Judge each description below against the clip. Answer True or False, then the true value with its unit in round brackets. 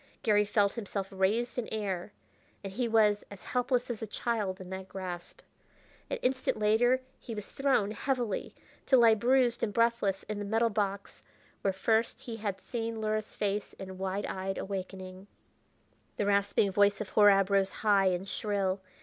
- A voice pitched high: True (205 Hz)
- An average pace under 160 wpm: False (165 wpm)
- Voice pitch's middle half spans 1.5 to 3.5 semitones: True (2.8 semitones)